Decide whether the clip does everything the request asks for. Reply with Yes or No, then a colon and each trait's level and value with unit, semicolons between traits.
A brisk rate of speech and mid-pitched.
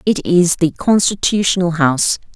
No: slow, 130 wpm; medium, 175 Hz